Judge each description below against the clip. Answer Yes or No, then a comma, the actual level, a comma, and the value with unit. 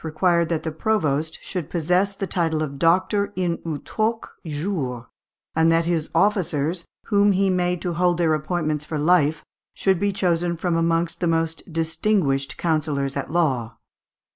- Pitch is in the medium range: Yes, medium, 165 Hz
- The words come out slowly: No, average, 155 wpm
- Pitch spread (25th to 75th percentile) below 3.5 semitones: Yes, average, 2.7 semitones